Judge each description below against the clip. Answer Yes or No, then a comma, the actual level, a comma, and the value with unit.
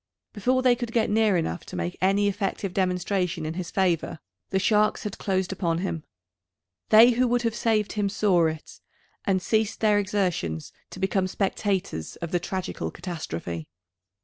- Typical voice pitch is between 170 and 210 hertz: Yes, high, 190 Hz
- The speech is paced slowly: No, average, 165 wpm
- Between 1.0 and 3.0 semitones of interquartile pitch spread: No, average, 3.4 semitones